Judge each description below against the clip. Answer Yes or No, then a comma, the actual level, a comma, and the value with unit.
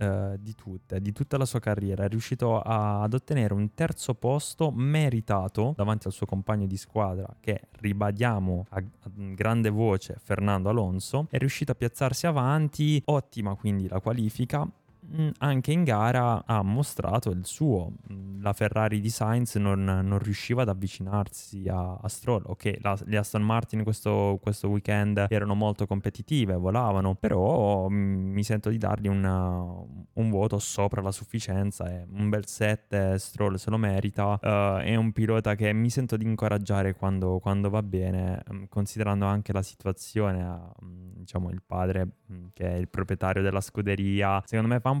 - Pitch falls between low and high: No, low, 105 Hz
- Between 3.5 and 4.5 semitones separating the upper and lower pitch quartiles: No, narrow, 2.5 semitones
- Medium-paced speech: Yes, average, 160 wpm